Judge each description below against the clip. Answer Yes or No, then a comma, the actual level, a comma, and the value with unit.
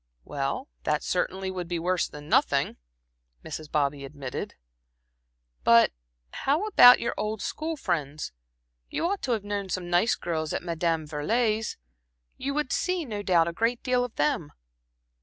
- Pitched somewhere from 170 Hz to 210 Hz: Yes, medium, 185 Hz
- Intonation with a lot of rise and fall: Yes, wide, 7.8 semitones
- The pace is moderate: Yes, average, 150 wpm